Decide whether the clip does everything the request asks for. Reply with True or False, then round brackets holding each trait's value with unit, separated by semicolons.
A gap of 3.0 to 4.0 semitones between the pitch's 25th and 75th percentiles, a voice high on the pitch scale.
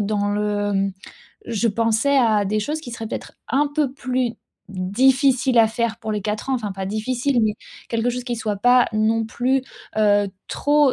True (3.5 semitones; 225 Hz)